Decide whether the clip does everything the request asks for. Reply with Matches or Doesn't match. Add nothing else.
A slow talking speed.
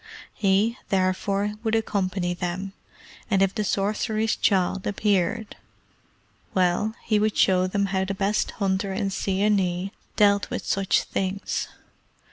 Matches